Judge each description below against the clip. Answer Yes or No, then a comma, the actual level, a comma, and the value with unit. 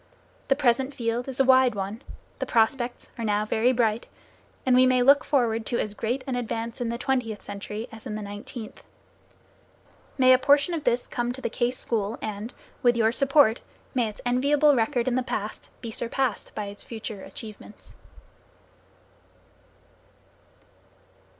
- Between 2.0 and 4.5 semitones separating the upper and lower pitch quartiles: Yes, average, 2.8 semitones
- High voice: Yes, high, 240 Hz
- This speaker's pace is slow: No, average, 165 wpm